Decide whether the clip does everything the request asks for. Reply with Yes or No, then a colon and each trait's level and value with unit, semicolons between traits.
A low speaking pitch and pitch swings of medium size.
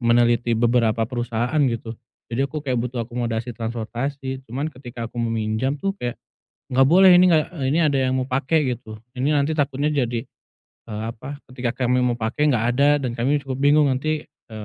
Yes: low, 125 Hz; average, 3.3 semitones